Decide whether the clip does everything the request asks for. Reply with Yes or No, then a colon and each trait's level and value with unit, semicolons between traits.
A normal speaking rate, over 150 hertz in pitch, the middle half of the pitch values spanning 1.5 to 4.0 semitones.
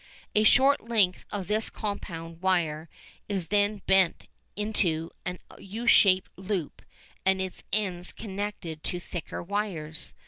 No: slow, 130 wpm; high, 190 Hz; average, 3.2 semitones